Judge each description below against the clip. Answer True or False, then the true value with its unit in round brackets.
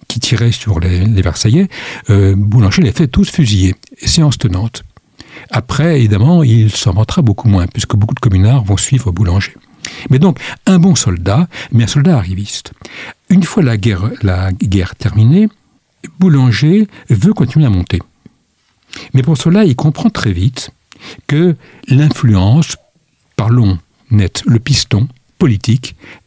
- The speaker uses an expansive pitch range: True (6.5 semitones)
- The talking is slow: True (140 wpm)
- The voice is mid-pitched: False (120 Hz)